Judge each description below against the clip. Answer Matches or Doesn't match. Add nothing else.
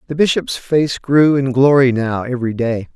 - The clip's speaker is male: Matches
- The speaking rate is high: Doesn't match